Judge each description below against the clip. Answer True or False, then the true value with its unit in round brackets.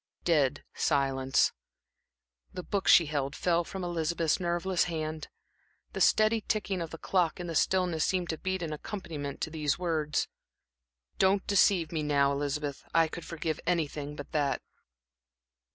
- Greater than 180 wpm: False (150 wpm)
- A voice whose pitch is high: False (165 Hz)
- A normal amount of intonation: True (3.2 semitones)